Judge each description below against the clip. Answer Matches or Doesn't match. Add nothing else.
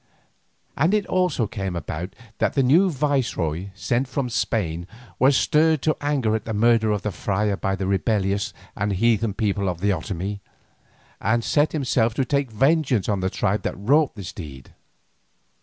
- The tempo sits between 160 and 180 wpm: Matches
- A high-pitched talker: Doesn't match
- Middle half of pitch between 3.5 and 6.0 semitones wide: Matches